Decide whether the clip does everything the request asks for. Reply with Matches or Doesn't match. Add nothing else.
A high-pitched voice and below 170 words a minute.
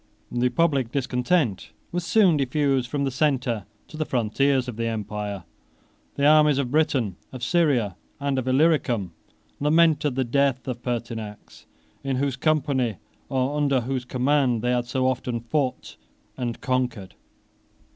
Doesn't match